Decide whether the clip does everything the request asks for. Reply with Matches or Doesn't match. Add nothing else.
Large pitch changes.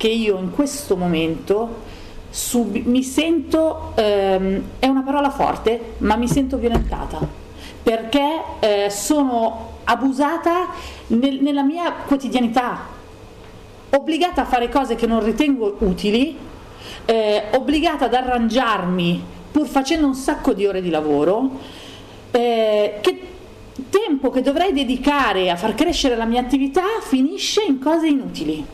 Doesn't match